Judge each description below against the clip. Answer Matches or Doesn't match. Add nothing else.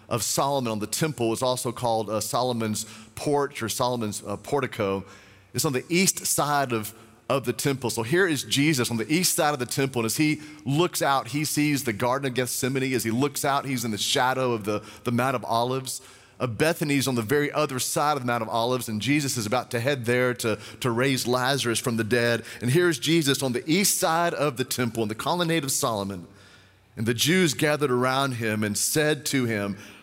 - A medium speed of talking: Doesn't match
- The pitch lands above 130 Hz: Doesn't match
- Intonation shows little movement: Doesn't match